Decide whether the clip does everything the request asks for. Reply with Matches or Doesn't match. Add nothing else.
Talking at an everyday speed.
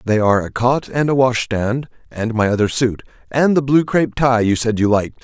Doesn't match